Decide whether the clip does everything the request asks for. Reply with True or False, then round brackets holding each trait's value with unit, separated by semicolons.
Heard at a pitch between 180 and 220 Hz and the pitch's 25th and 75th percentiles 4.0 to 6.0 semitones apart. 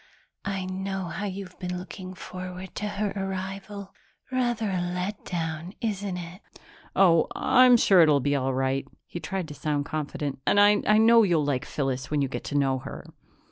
True (185 Hz; 4.6 semitones)